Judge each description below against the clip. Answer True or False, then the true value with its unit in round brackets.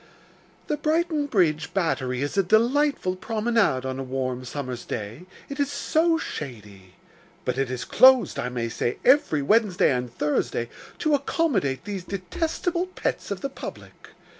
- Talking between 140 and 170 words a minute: True (150 wpm)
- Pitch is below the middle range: False (185 Hz)